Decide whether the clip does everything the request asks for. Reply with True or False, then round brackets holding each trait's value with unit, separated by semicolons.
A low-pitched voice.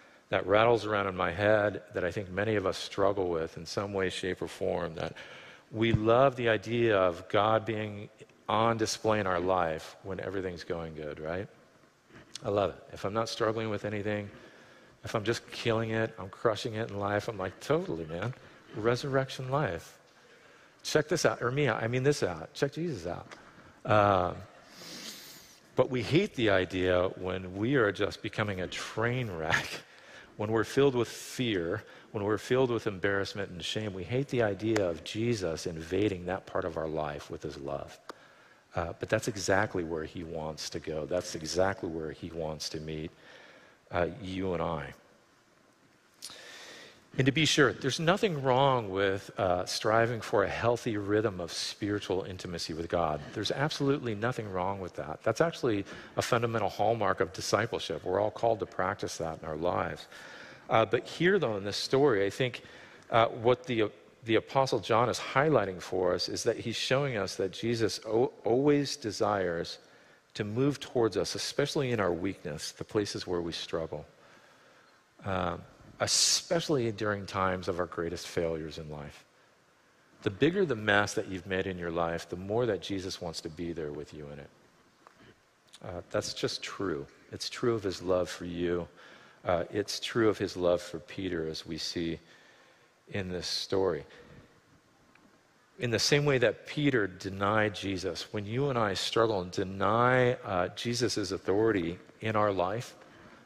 True (105 Hz)